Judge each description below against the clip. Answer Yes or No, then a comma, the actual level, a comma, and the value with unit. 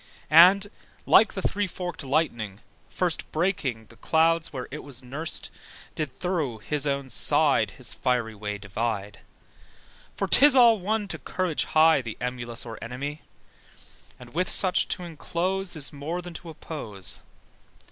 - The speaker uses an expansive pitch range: Yes, wide, 6.7 semitones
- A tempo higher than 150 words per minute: No, average, 145 wpm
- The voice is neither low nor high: Yes, medium, 150 Hz